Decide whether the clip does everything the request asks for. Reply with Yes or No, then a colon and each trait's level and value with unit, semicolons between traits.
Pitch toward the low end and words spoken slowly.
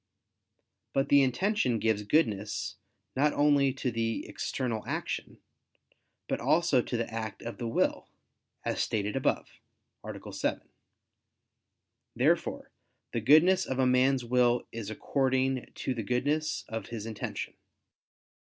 Yes: low, 125 Hz; slow, 125 wpm